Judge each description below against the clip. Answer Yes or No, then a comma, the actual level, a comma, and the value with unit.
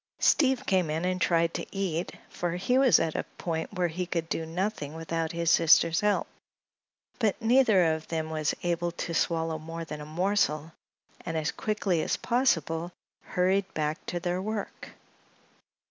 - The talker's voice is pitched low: No, medium, 170 Hz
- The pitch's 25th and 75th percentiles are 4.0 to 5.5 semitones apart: No, average, 3.0 semitones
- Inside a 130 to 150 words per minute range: No, average, 165 wpm